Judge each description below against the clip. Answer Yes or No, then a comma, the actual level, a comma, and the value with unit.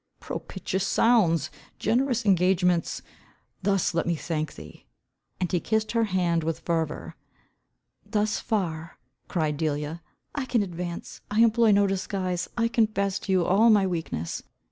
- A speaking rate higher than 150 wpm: No, average, 140 wpm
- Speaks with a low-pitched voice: No, medium, 185 Hz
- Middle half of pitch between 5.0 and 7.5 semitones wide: No, average, 4.3 semitones